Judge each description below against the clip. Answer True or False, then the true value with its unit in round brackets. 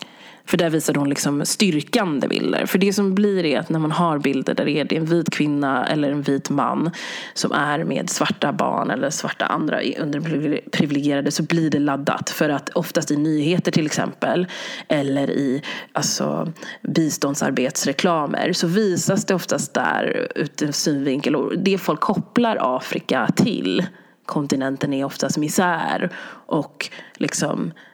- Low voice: False (155 Hz)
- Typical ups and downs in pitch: True (3.7 semitones)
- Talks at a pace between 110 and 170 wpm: True (150 wpm)